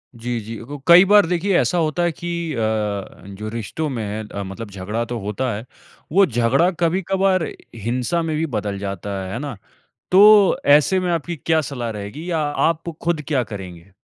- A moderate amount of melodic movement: No, wide, 8.0 semitones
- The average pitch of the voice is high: No, medium, 140 Hz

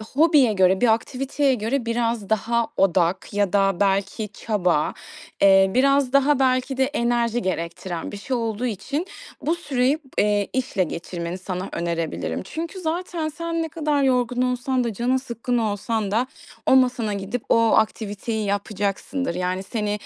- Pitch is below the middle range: No, high, 230 Hz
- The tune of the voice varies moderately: Yes, average, 5.0 semitones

